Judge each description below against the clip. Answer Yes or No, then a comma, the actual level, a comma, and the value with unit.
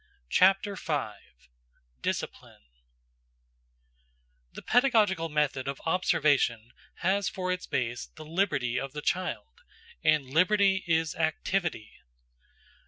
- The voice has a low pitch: No, medium, 160 Hz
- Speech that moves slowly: Yes, slow, 100 wpm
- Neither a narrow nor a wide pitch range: No, wide, 5.7 semitones